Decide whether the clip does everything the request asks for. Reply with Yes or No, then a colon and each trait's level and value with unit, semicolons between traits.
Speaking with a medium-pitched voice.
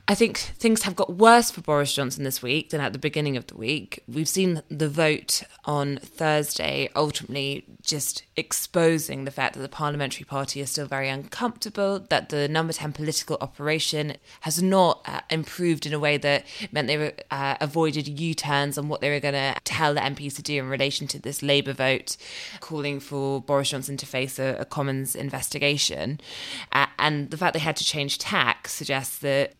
Yes: medium, 145 Hz